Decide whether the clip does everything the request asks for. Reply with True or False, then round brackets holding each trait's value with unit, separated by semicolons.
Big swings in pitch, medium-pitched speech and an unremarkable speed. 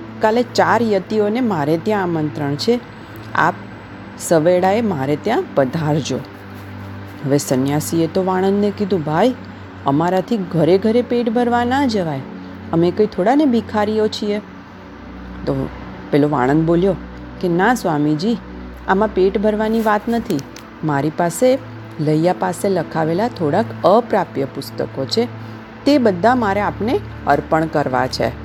True (7.5 semitones; 175 Hz; 115 wpm)